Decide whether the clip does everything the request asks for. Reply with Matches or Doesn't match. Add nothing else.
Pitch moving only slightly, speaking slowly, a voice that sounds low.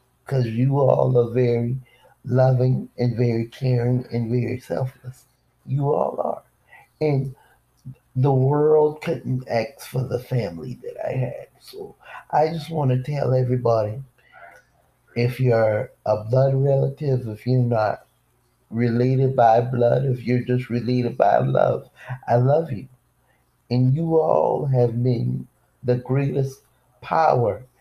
Matches